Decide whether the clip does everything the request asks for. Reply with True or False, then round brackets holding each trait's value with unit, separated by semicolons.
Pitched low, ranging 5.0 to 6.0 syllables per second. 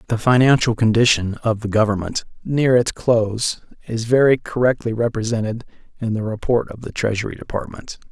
True (115 Hz; 5.4 syllables/s)